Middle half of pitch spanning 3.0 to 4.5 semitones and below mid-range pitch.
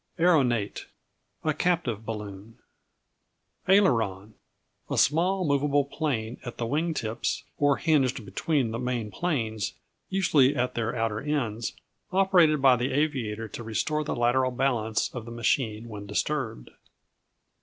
No: average, 5.3 semitones; low, 125 Hz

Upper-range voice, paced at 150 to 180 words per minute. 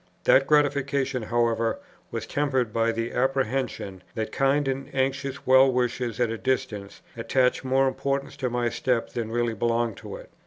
No: low, 125 Hz; average, 160 wpm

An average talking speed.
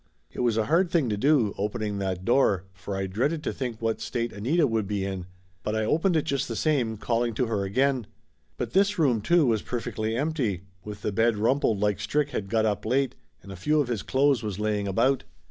No: fast, 225 wpm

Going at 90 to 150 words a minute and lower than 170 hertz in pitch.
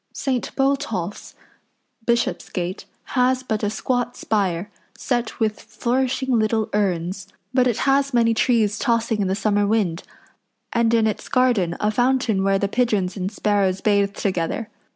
No: average, 145 wpm; high, 215 Hz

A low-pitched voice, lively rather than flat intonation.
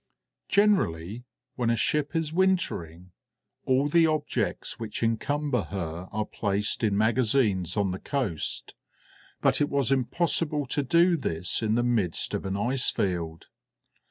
Yes: low, 120 Hz; wide, 7.0 semitones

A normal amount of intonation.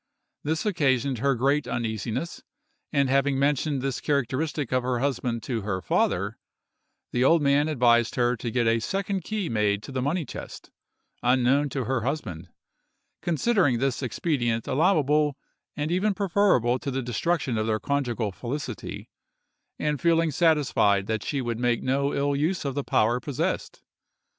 Yes: average, 3.9 semitones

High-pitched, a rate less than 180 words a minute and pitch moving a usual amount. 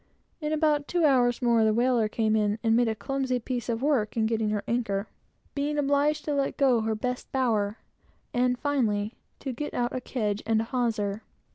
No: high, 240 Hz; average, 195 wpm; average, 3.8 semitones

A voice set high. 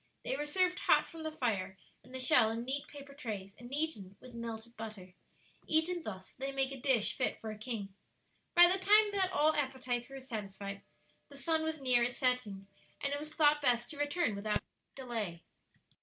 Yes: very high, 255 Hz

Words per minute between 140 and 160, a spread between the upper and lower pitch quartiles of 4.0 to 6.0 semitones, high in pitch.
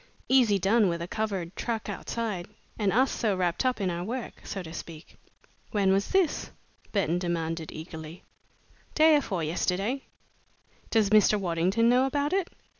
Yes: average, 155 wpm; average, 5.2 semitones; high, 200 Hz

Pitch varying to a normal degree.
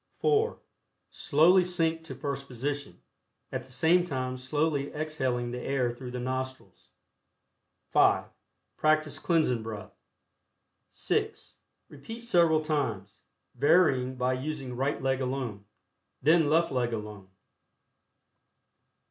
Yes: average, 3.8 semitones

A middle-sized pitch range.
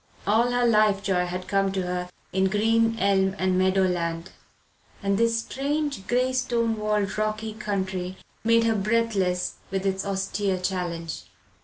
Yes: average, 3.3 semitones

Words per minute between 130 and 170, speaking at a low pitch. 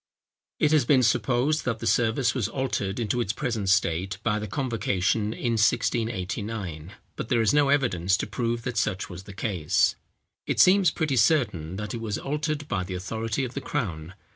No: average, 185 wpm; low, 115 Hz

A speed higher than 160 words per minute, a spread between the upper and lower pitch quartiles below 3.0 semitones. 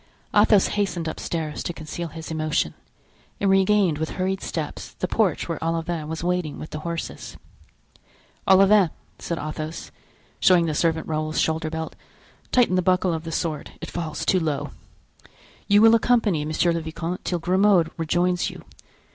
No: average, 155 wpm; narrow, 2.6 semitones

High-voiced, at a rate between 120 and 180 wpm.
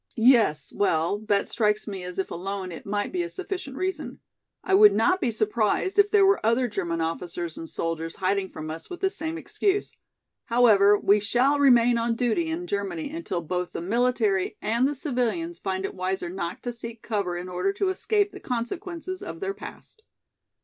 No: high, 230 Hz; average, 190 wpm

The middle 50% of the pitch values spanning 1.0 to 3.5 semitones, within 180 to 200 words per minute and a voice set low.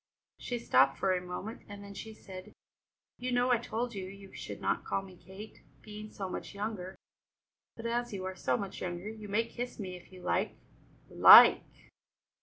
No: average, 3.1 semitones; average, 190 wpm; high, 200 Hz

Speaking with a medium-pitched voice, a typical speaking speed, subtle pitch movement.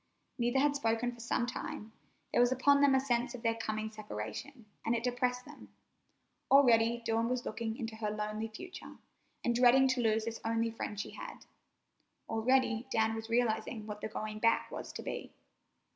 No: high, 230 Hz; average, 180 wpm; narrow, 2.1 semitones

